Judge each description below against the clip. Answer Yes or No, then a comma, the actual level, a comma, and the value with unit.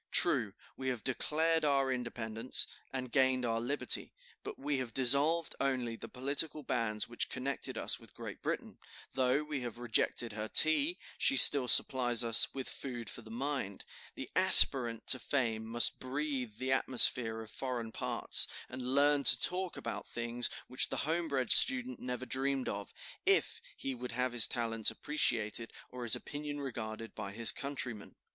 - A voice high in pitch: No, low, 130 Hz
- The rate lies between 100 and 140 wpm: No, average, 165 wpm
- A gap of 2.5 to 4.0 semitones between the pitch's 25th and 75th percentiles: Yes, average, 3.2 semitones